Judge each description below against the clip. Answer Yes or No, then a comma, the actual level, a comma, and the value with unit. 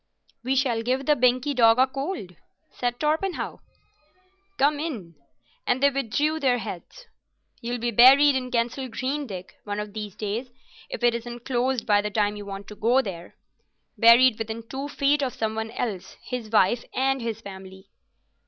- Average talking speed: Yes, average, 170 wpm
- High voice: Yes, high, 240 Hz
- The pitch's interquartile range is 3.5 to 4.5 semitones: Yes, average, 3.8 semitones